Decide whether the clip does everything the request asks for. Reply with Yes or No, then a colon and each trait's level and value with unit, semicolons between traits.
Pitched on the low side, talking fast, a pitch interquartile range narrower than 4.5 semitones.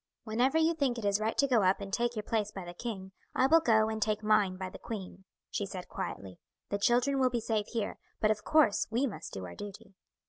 No: high, 215 Hz; fast, 245 wpm; average, 3.4 semitones